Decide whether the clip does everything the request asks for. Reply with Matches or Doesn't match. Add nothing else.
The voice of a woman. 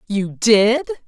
Matches